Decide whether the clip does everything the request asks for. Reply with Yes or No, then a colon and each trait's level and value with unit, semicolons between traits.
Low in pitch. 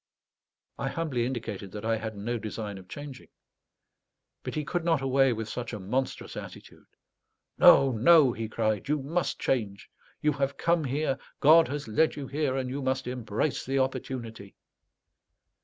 Yes: low, 130 Hz